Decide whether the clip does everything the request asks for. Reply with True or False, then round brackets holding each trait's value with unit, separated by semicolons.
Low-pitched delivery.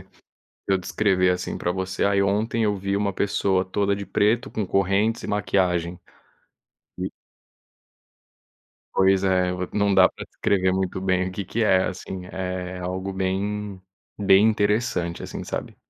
True (95 Hz)